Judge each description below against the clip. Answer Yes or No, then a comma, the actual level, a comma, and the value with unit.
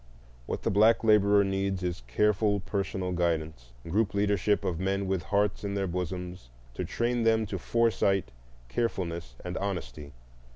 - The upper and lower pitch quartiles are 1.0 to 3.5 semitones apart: Yes, average, 2.9 semitones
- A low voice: Yes, very low, 95 Hz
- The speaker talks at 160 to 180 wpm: No, average, 150 wpm